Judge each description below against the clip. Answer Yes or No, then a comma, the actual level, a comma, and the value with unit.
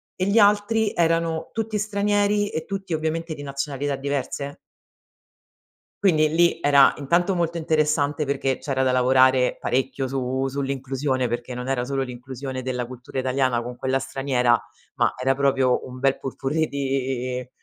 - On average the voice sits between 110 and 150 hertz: Yes, low, 135 Hz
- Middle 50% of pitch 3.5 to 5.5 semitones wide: Yes, average, 3.8 semitones